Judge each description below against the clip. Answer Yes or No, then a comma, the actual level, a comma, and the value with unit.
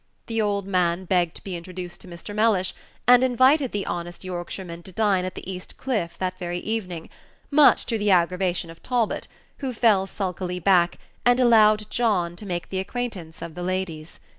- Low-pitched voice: No, high, 190 Hz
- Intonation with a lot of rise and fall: No, average, 3.8 semitones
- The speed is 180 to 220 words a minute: Yes, average, 185 wpm